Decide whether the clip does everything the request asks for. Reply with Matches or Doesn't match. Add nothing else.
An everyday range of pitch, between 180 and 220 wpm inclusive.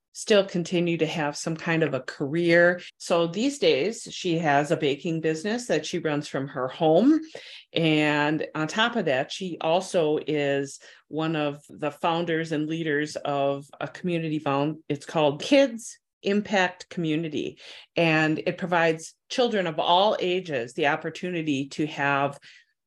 Doesn't match